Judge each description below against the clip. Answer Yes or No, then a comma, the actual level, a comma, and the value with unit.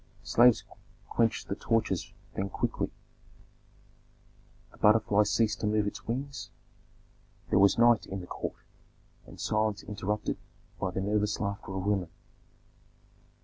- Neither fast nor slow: No, slow, 125 wpm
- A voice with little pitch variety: Yes, narrow, 2.0 semitones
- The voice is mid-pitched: No, low, 105 Hz